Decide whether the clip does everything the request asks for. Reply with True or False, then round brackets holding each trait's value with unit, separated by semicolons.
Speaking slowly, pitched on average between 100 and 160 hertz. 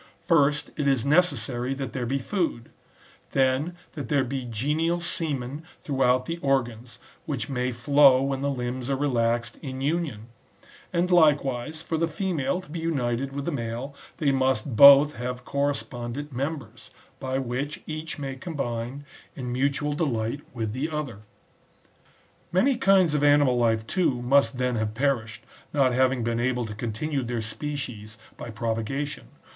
False (155 wpm; 135 Hz)